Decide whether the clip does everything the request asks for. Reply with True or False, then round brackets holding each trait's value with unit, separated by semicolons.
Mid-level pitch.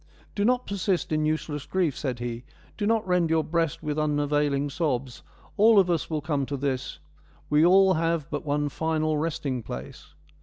True (155 Hz)